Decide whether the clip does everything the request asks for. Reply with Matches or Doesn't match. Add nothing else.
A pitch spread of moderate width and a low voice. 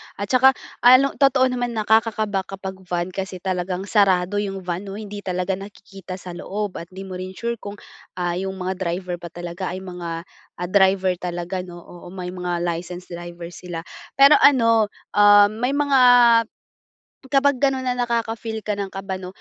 Doesn't match